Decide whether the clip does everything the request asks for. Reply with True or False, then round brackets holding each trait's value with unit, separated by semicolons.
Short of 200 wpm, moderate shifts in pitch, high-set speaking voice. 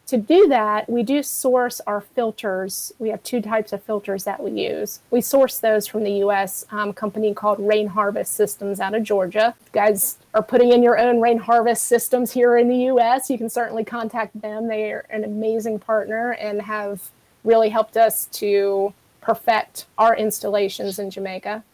False (180 wpm; 2.2 semitones; 220 Hz)